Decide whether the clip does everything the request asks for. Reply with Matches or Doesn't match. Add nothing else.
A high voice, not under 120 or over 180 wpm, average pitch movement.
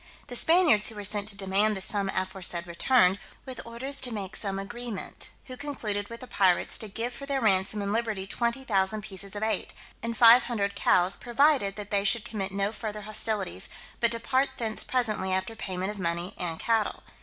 Doesn't match